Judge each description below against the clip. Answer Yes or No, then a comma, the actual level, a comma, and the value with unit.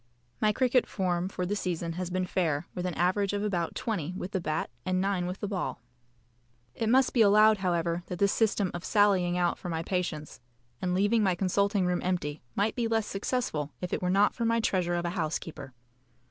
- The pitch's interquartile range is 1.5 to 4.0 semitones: Yes, average, 2.8 semitones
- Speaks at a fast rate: Yes, fast, 210 wpm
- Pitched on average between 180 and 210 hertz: Yes, medium, 185 Hz